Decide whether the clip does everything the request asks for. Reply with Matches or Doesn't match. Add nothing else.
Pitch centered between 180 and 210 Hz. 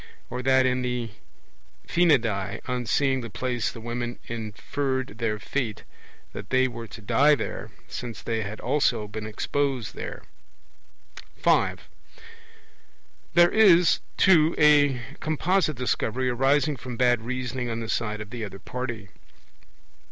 Doesn't match